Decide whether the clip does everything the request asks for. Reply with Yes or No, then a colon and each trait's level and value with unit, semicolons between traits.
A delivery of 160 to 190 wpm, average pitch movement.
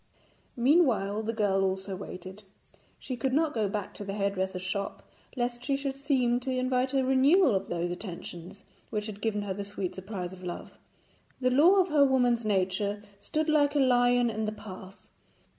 Yes: average, 180 wpm; average, 5.0 semitones